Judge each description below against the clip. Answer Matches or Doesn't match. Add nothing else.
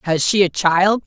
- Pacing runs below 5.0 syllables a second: Matches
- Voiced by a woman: Matches